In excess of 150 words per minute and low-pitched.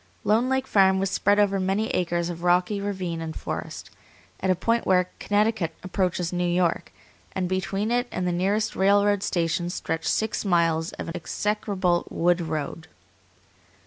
No: average, 160 wpm; medium, 185 Hz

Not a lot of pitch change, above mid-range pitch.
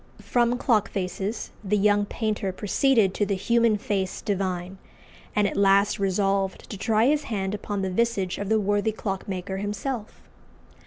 Yes: narrow, 2.1 semitones; high, 205 Hz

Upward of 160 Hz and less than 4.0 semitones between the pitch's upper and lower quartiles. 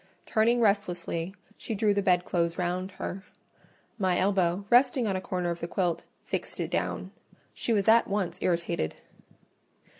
Yes: high, 190 Hz; average, 2.8 semitones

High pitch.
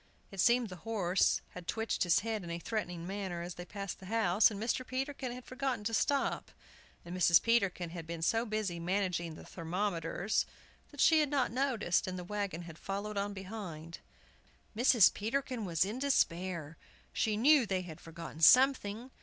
Yes: high, 200 Hz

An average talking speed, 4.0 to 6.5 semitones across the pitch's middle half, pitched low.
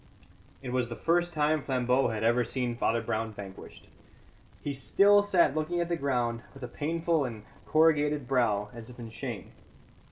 Yes: average, 170 wpm; average, 4.9 semitones; low, 130 Hz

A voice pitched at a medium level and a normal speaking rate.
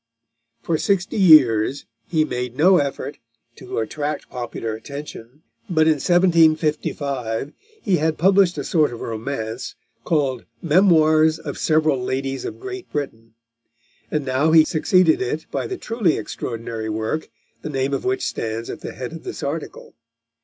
Yes: medium, 150 Hz; average, 150 wpm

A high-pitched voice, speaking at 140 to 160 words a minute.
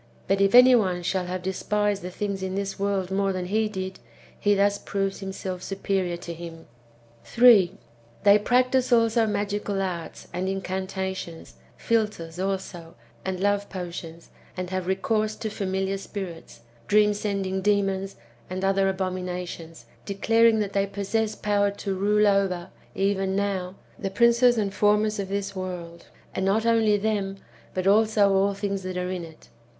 Yes: high, 195 Hz; average, 155 wpm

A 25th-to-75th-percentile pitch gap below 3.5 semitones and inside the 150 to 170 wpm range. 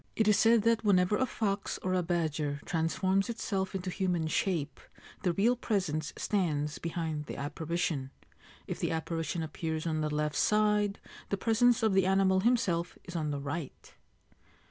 No: average, 4.3 semitones; average, 165 wpm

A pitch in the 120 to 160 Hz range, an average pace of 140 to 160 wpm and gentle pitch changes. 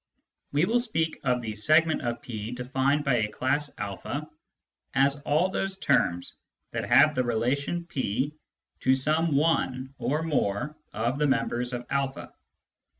No: low, 135 Hz; average, 155 wpm; average, 3.9 semitones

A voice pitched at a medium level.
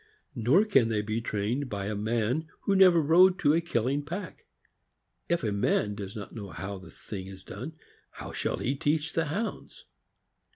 No: low, 125 Hz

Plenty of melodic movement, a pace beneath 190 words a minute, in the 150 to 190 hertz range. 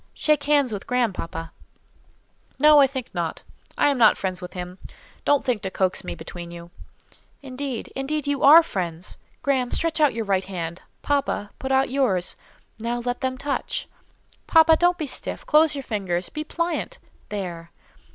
No: wide, 7.5 semitones; average, 165 wpm; very high, 250 Hz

